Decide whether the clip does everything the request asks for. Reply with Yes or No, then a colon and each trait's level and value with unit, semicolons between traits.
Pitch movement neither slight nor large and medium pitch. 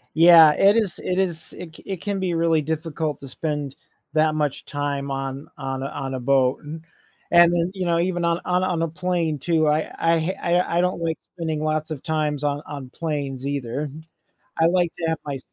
Yes: average, 3.1 semitones; medium, 160 Hz